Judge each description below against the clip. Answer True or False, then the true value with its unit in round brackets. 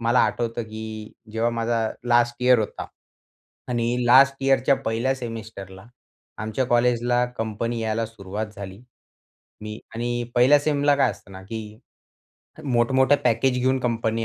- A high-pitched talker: False (115 Hz)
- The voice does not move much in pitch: True (2.1 semitones)